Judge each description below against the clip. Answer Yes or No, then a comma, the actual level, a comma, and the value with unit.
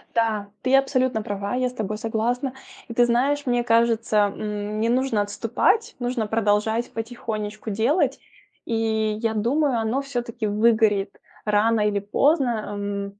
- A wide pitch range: No, average, 2.8 semitones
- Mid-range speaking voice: No, high, 225 Hz